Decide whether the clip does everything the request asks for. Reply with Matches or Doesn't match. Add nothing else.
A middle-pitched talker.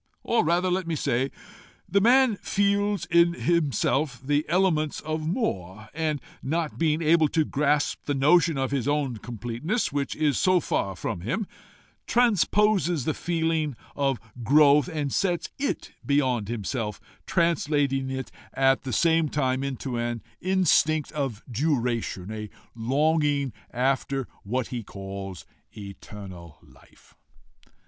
Matches